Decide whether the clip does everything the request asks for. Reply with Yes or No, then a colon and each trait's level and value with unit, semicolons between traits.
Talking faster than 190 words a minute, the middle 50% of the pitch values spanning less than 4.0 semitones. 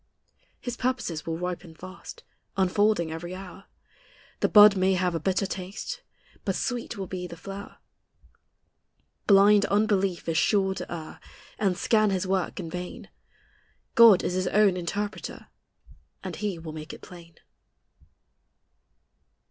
No: slow, 135 wpm; average, 2.7 semitones